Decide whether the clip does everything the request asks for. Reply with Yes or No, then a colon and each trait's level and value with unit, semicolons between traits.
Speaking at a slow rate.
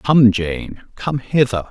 Yes: slow, 105 wpm